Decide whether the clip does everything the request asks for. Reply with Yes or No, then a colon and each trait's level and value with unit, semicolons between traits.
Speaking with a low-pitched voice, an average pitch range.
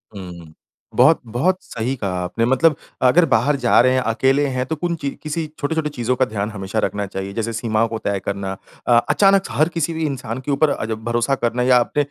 Yes: low, 125 Hz; average, 4.9 semitones